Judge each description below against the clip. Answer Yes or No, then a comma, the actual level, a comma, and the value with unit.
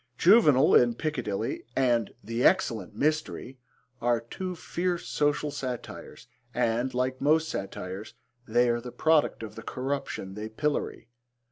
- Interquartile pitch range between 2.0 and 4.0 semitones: No, average, 4.7 semitones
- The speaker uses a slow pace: Yes, slow, 130 wpm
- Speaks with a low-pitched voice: Yes, low, 125 Hz